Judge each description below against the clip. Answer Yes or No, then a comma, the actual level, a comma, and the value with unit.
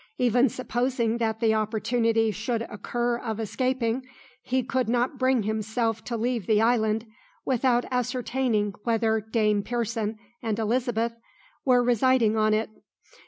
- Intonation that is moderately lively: No, narrow, 2.1 semitones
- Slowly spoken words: Yes, slow, 130 wpm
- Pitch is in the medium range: No, high, 230 Hz